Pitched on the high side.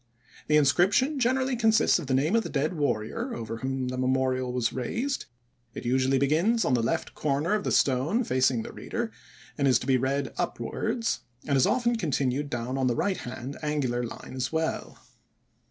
No: medium, 140 Hz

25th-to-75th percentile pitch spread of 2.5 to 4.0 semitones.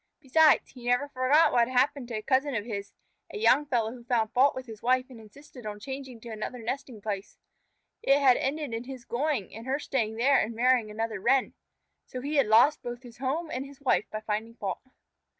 Yes: average, 3.4 semitones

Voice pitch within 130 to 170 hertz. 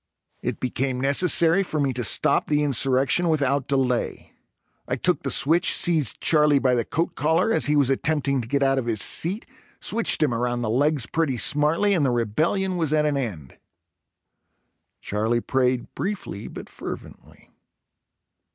Yes: medium, 140 Hz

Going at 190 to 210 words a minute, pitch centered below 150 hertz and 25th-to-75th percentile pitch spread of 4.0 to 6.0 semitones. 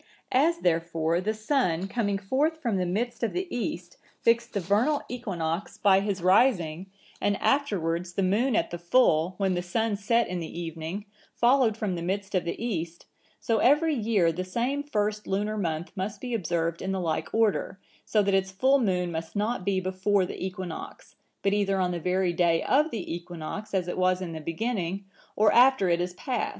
No: average, 195 wpm; high, 195 Hz; average, 4.5 semitones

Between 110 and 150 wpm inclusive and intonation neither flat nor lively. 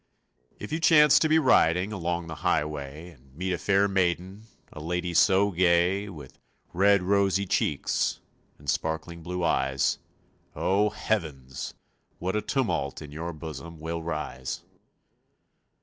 Yes: slow, 135 wpm; average, 4.0 semitones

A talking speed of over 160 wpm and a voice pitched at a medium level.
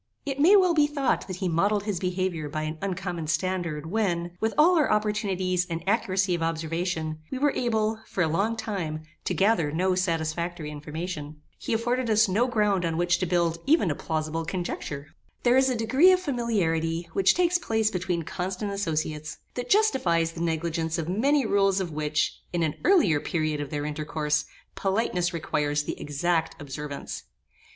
Yes: average, 175 wpm; medium, 180 Hz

